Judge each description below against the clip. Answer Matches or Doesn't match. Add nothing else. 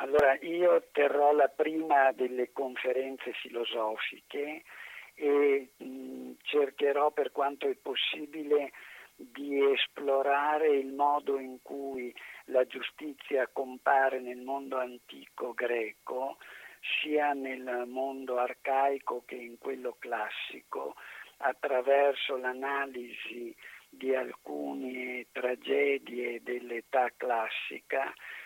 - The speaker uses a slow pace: Matches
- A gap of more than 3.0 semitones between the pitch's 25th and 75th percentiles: Doesn't match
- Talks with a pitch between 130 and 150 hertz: Matches